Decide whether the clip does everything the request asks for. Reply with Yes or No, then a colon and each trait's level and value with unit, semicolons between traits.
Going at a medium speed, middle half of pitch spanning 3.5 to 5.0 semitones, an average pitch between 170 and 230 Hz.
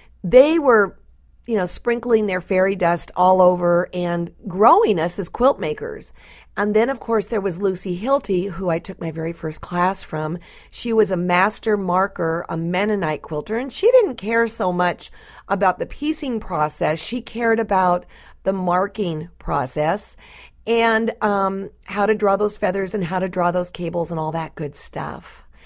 Yes: average, 175 wpm; average, 4.0 semitones; high, 190 Hz